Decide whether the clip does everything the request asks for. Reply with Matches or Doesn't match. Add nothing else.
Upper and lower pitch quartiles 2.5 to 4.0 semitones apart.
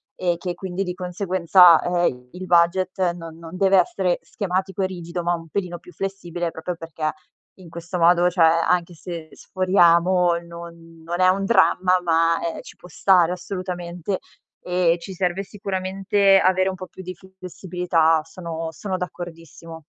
Doesn't match